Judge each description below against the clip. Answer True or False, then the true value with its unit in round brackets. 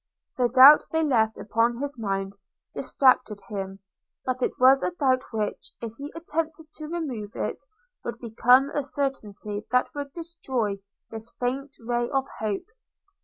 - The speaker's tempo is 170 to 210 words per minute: False (150 wpm)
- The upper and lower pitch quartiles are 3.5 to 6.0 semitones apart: True (4.4 semitones)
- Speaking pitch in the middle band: False (250 Hz)